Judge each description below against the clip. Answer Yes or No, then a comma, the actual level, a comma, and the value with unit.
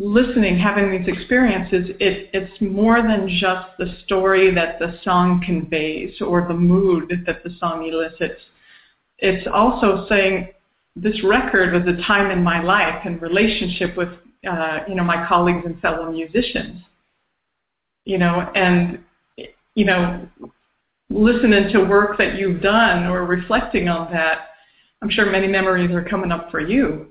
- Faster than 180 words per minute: No, average, 150 wpm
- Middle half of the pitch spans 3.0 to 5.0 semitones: No, narrow, 2.5 semitones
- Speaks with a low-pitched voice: No, medium, 185 Hz